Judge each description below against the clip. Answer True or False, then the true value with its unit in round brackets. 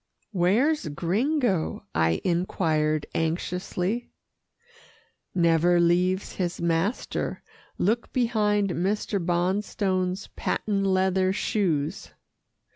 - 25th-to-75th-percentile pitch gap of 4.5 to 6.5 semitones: False (3.2 semitones)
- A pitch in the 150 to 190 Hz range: True (185 Hz)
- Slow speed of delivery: True (75 wpm)